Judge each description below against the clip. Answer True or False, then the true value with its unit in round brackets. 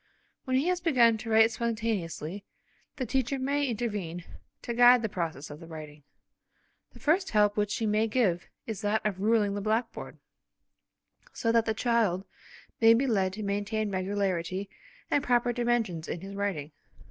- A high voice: True (215 Hz)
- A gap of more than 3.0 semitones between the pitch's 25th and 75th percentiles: True (3.7 semitones)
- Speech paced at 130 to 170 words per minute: True (165 wpm)